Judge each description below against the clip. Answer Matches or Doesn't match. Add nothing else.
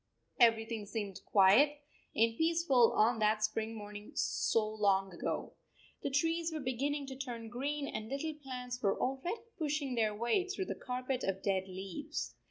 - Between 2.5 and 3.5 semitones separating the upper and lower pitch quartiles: Doesn't match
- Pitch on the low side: Doesn't match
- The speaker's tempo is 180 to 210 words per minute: Doesn't match